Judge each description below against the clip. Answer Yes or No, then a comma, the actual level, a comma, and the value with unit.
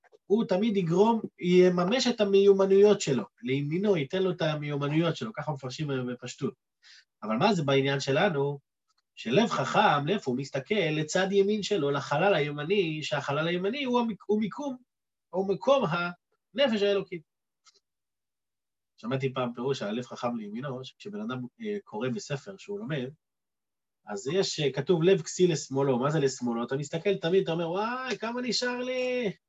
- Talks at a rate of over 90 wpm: Yes, average, 145 wpm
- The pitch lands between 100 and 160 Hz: No, medium, 185 Hz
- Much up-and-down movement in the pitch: Yes, wide, 6.5 semitones